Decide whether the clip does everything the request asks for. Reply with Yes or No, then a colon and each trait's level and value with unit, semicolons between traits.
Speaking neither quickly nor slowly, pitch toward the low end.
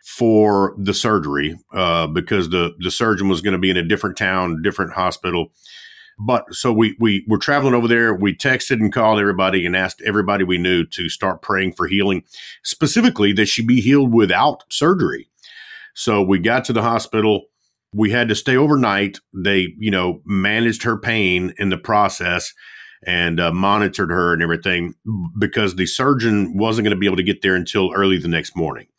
Yes: average, 185 wpm; low, 100 Hz